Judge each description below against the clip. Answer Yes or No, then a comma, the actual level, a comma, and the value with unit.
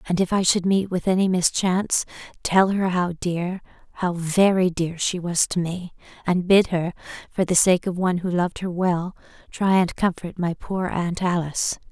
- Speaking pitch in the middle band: Yes, medium, 180 Hz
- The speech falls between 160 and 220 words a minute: Yes, average, 190 wpm